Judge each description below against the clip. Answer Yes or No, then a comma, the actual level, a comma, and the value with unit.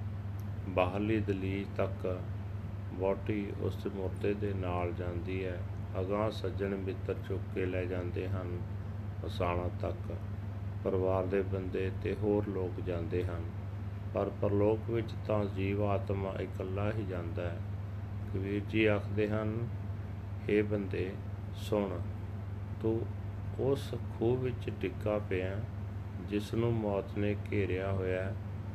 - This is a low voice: Yes, low, 100 Hz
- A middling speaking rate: Yes, average, 120 wpm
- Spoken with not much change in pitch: Yes, narrow, 1.1 semitones